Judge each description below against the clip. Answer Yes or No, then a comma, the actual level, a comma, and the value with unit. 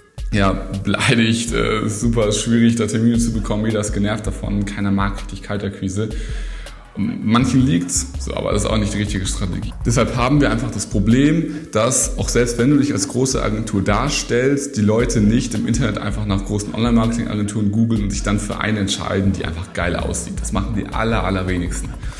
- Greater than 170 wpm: Yes, average, 185 wpm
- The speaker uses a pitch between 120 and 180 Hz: No, low, 105 Hz